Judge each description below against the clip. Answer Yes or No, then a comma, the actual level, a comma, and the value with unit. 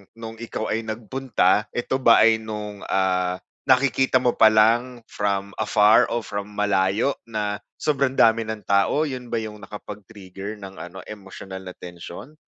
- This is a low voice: Yes, low, 110 Hz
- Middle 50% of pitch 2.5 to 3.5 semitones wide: Yes, average, 2.9 semitones